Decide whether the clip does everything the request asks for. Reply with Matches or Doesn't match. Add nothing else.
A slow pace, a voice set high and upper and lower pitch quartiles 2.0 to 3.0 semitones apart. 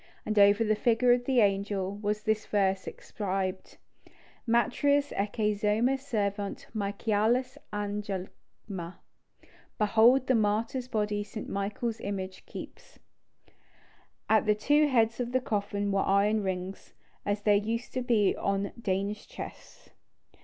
Matches